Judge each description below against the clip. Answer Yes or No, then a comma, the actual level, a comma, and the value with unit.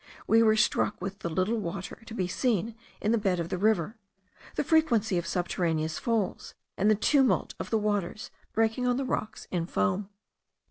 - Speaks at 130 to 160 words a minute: No, average, 185 wpm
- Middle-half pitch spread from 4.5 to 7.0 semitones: No, average, 4.1 semitones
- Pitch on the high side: Yes, high, 210 Hz